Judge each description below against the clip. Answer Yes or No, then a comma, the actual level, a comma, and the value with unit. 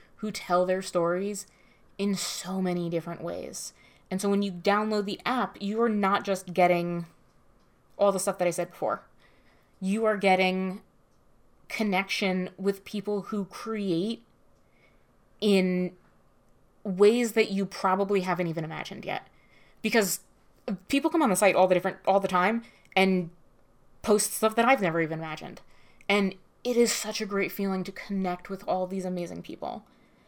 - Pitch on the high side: Yes, high, 195 Hz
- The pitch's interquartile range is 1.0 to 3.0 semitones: Yes, narrow, 2.4 semitones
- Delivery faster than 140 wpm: Yes, average, 155 wpm